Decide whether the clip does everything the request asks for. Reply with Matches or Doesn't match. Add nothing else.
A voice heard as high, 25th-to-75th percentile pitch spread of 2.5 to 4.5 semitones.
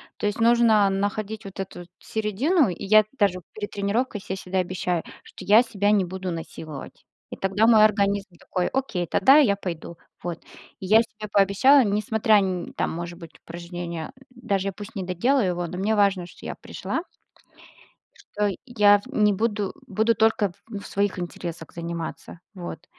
Matches